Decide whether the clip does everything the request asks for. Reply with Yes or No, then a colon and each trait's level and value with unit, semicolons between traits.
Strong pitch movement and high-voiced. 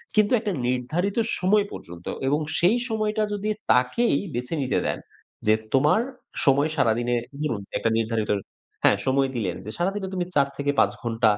No: wide, 8.3 semitones; medium, 140 Hz